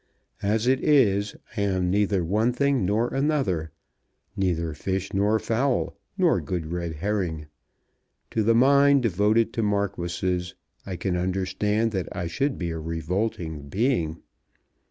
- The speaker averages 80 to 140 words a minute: Yes, slow, 135 wpm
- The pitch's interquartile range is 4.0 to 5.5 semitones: Yes, average, 4.4 semitones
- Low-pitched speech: Yes, low, 100 Hz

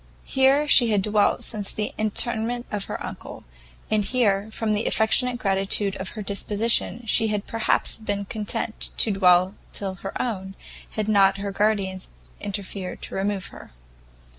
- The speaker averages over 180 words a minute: No, average, 155 wpm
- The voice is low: No, high, 210 Hz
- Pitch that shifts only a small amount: Yes, narrow, 2.2 semitones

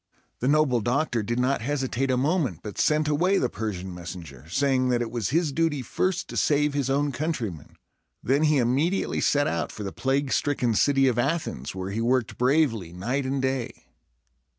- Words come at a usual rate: Yes, average, 185 wpm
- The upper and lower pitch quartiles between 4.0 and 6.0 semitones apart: Yes, average, 4.3 semitones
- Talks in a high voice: No, low, 130 Hz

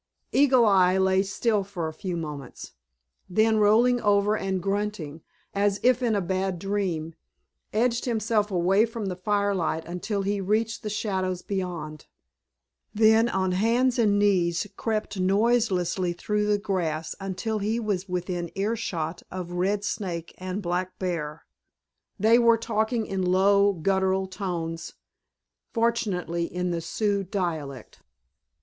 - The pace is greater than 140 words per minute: No, slow, 135 wpm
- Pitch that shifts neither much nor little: Yes, average, 3.1 semitones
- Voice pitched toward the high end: Yes, high, 195 Hz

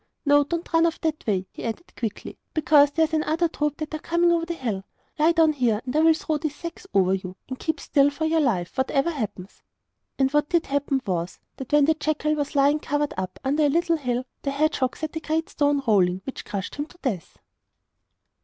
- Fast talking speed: Yes, fast, 220 wpm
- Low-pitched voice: No, very high, 290 Hz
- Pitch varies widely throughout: No, average, 3.9 semitones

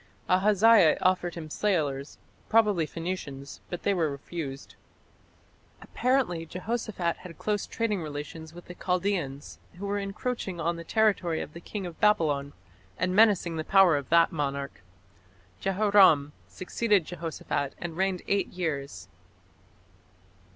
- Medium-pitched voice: Yes, medium, 175 Hz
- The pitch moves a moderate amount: Yes, average, 4.3 semitones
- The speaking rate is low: Yes, slow, 130 wpm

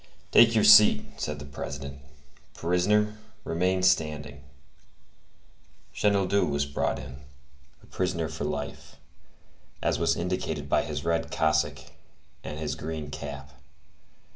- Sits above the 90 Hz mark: No, very low, 80 Hz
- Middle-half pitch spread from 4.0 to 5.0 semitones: Yes, average, 4.4 semitones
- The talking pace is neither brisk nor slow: No, slow, 115 wpm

